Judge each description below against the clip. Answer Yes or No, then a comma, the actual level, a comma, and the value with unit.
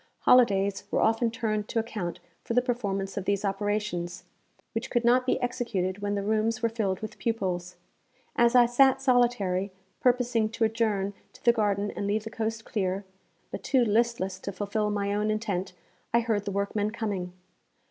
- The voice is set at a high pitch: Yes, high, 215 Hz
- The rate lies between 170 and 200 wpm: Yes, average, 175 wpm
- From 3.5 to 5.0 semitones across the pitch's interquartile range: No, average, 2.8 semitones